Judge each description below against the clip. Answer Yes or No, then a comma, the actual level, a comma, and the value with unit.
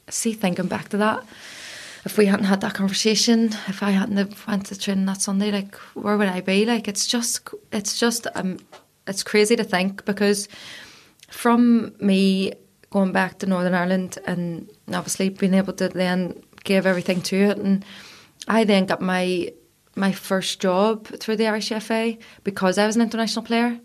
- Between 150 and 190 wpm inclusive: Yes, average, 180 wpm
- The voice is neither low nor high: No, high, 200 Hz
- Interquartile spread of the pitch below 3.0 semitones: Yes, narrow, 2.4 semitones